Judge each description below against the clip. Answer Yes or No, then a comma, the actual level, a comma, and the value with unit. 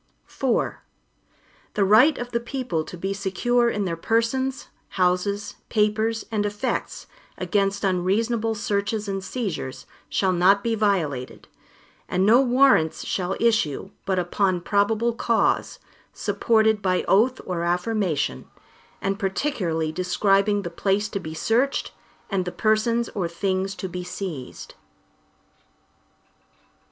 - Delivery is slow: Yes, slow, 125 wpm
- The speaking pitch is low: No, high, 200 Hz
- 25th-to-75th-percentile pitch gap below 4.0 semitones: Yes, average, 3.6 semitones